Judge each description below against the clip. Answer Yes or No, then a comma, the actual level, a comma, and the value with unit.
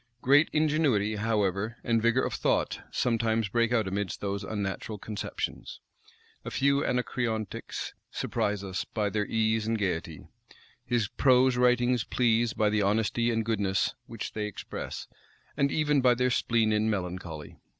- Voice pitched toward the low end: Yes, low, 110 Hz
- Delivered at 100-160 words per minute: Yes, average, 145 wpm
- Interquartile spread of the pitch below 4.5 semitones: Yes, average, 2.9 semitones